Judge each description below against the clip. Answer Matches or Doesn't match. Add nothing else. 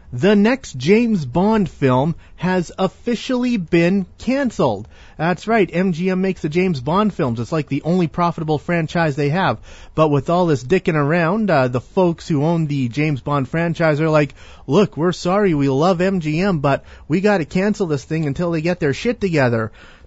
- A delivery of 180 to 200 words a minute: Matches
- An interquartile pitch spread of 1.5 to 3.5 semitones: Doesn't match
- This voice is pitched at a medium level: Matches